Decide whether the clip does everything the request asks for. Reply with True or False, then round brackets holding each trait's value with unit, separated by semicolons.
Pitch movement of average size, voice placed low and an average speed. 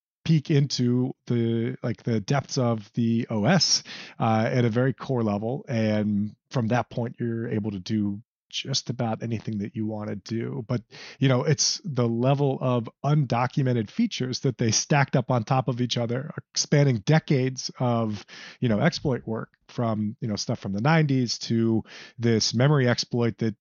True (3.1 semitones; 120 Hz; 175 wpm)